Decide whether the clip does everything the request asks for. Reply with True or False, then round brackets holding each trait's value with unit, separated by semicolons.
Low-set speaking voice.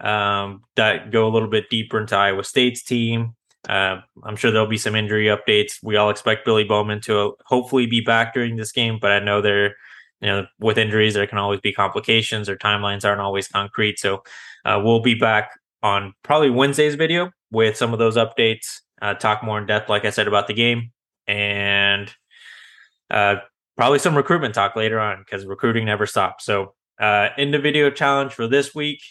True (110 Hz)